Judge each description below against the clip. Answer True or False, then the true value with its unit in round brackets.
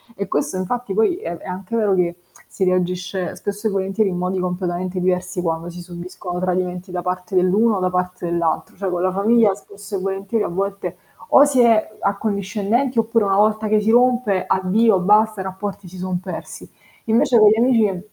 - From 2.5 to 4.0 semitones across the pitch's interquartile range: True (2.9 semitones)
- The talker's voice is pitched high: True (195 Hz)